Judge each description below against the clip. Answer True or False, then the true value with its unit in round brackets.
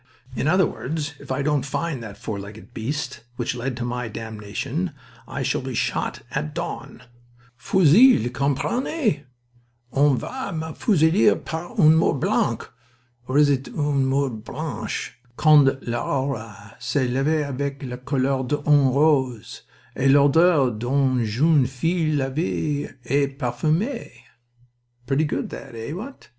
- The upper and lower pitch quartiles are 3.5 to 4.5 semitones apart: True (3.8 semitones)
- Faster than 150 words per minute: False (135 wpm)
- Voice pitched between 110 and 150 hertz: True (140 Hz)